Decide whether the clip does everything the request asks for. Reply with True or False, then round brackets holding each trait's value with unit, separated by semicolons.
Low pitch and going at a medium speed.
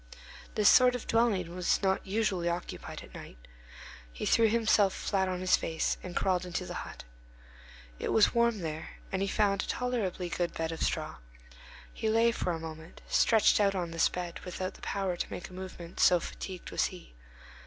False (185 Hz; 190 wpm)